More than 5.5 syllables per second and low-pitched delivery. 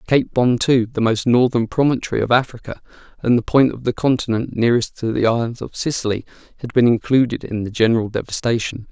Yes: 6.0 syllables/s; low, 120 Hz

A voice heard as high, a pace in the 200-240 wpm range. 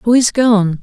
Yes: high, 220 Hz; fast, 215 wpm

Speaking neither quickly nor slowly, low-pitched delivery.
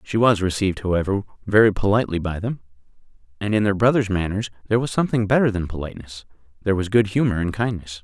Yes: average, 185 wpm; low, 100 Hz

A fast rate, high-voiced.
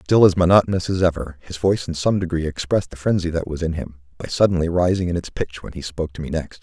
No: fast, 260 wpm; very low, 85 Hz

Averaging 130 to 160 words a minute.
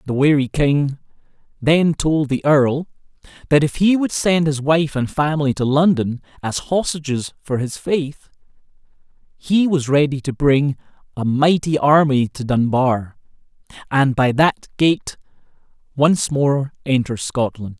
Yes: average, 140 wpm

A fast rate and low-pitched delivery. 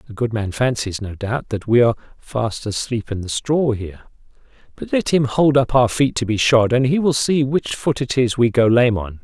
Yes: fast, 240 wpm; low, 120 Hz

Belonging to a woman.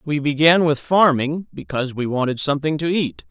No: male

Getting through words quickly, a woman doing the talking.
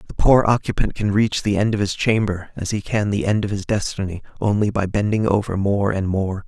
No: fast, 230 wpm; male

